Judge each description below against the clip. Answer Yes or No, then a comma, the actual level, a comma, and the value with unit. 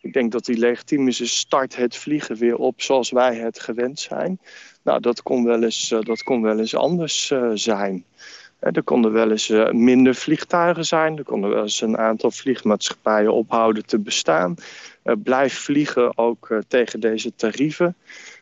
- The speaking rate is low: No, average, 160 wpm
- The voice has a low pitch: Yes, low, 120 Hz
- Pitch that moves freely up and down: No, average, 3.3 semitones